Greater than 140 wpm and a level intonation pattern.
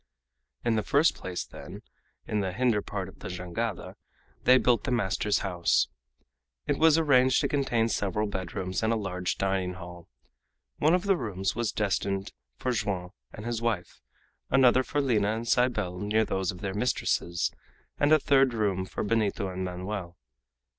No: average, 165 wpm; average, 4.7 semitones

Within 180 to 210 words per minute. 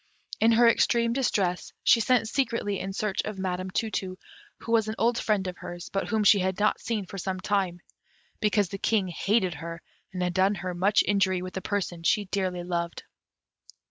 Yes: average, 200 wpm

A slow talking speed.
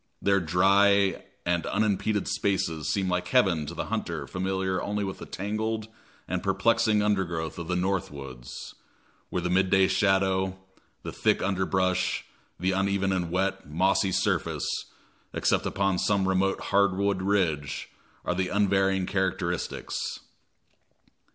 Yes: slow, 130 wpm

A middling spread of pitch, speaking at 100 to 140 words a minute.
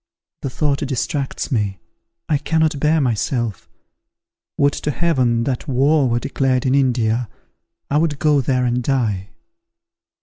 Yes: average, 3.3 semitones; slow, 135 wpm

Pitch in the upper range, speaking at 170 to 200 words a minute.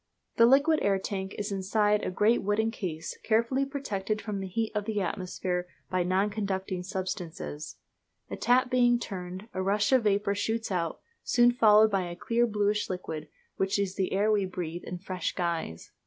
Yes: high, 200 Hz; average, 185 wpm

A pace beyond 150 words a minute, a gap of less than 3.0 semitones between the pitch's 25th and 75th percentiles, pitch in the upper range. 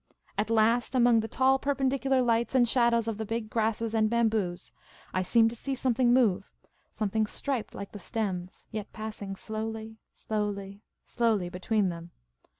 Yes: average, 160 wpm; narrow, 2.4 semitones; high, 220 Hz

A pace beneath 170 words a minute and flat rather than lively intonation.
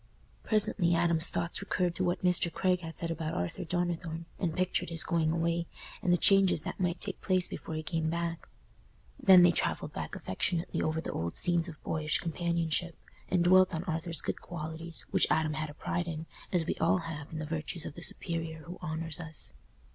No: average, 200 wpm; narrow, 1.7 semitones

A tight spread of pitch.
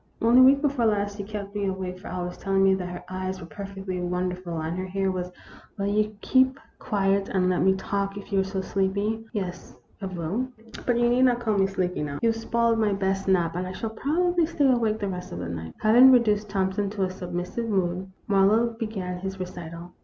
No: average, 3.2 semitones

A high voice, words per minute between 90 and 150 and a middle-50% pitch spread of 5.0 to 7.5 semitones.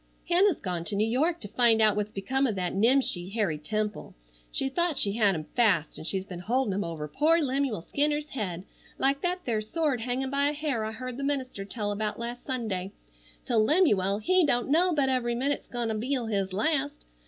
No: high, 235 Hz; fast, 205 wpm; wide, 5.5 semitones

